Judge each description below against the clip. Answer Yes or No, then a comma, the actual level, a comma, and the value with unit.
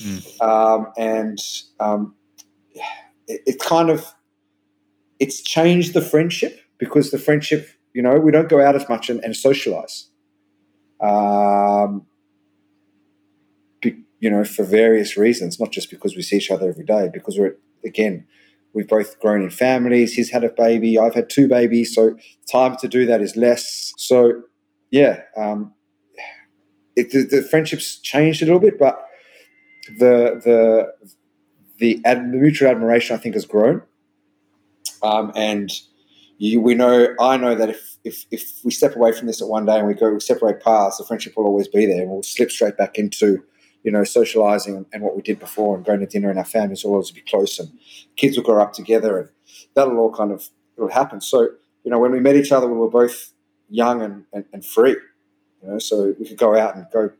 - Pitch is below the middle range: Yes, low, 110 Hz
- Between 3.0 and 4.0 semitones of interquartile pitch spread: Yes, average, 3.5 semitones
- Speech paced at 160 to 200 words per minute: Yes, average, 190 wpm